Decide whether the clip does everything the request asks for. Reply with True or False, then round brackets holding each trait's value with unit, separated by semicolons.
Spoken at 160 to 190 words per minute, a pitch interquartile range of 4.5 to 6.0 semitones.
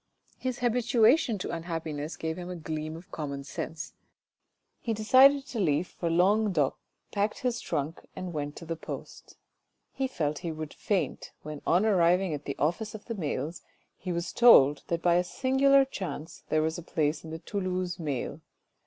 True (175 wpm; 5.6 semitones)